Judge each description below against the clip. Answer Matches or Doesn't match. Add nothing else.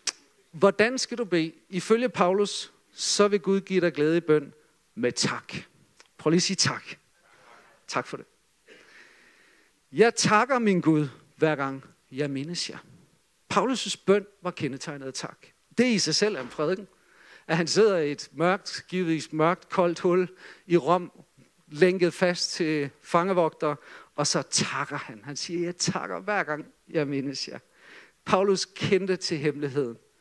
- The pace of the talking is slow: Doesn't match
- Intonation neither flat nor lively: Matches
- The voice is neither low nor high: Matches